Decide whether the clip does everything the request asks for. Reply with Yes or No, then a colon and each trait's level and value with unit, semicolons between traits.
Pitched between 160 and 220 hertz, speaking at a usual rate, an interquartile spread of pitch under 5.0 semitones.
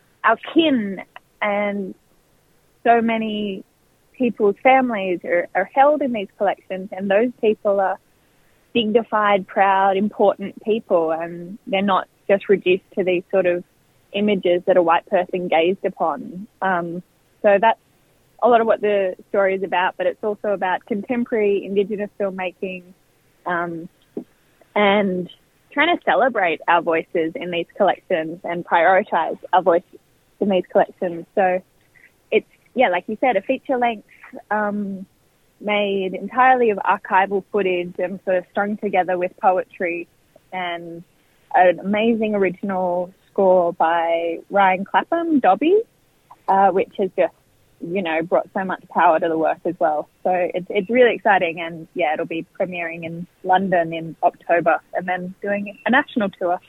Yes: high, 190 Hz; average, 145 wpm; average, 2.9 semitones